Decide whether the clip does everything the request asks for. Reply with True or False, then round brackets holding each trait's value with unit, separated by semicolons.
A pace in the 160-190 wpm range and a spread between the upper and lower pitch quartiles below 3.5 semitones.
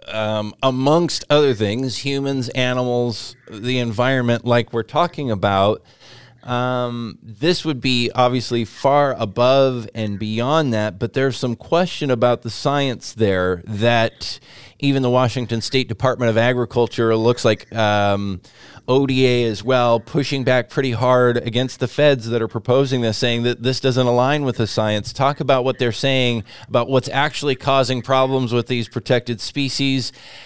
False (150 wpm; 2.4 semitones)